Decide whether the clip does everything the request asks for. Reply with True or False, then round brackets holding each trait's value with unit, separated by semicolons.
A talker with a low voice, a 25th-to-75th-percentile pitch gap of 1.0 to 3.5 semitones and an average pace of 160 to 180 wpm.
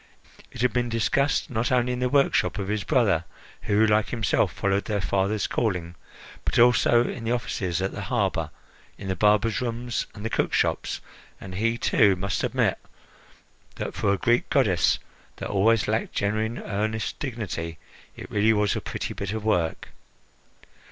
True (110 Hz; 3.0 semitones; 165 wpm)